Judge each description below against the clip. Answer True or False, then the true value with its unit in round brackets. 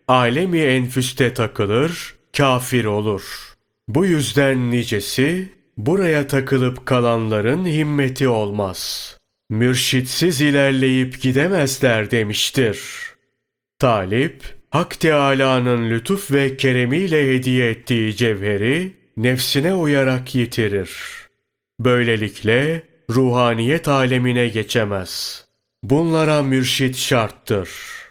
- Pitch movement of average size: True (3.1 semitones)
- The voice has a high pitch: False (130 Hz)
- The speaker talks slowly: True (75 wpm)